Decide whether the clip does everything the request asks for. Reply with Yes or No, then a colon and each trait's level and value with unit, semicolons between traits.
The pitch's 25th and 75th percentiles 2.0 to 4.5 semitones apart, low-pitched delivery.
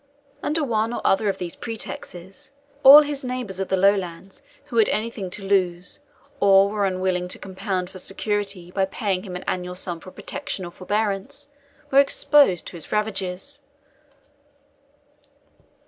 No: average, 3.5 semitones; high, 195 Hz